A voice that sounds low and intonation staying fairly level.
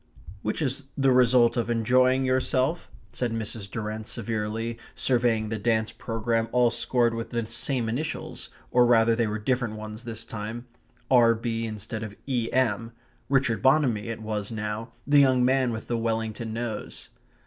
Yes: low, 115 Hz; narrow, 2.2 semitones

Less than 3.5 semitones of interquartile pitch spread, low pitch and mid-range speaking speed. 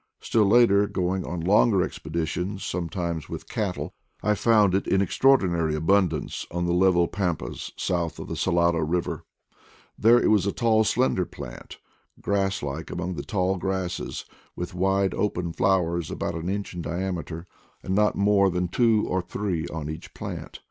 Yes: average, 2.7 semitones; very low, 90 Hz; average, 160 wpm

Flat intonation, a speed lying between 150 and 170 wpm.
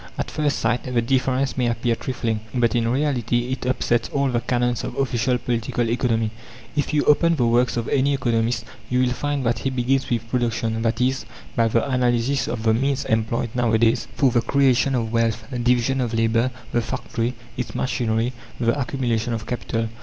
No: narrow, 2.1 semitones; average, 185 wpm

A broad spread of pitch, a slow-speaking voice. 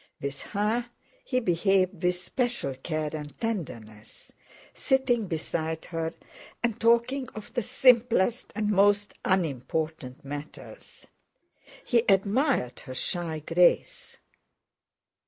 Yes: wide, 6.7 semitones; slow, 100 wpm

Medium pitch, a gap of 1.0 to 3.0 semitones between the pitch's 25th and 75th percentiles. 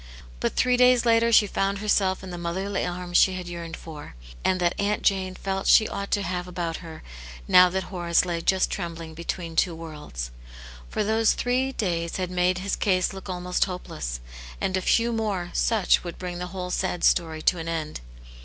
Yes: medium, 180 Hz; narrow, 2.6 semitones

